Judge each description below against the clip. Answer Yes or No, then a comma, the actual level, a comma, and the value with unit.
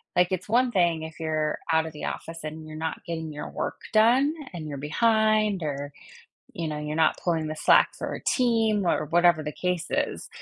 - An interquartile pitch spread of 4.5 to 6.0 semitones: Yes, average, 5.0 semitones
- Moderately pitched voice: Yes, medium, 165 Hz